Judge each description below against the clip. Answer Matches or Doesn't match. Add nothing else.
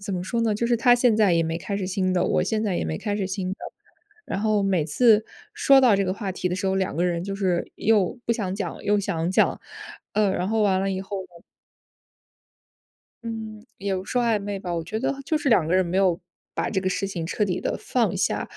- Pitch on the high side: Matches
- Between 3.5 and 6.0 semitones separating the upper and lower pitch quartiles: Doesn't match